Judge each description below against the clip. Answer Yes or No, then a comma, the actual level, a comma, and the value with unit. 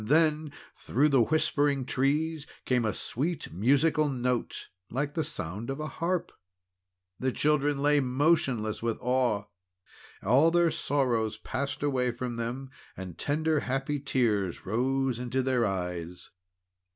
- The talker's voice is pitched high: No, low, 135 Hz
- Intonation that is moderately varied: Yes, average, 3.8 semitones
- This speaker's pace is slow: Yes, slow, 130 wpm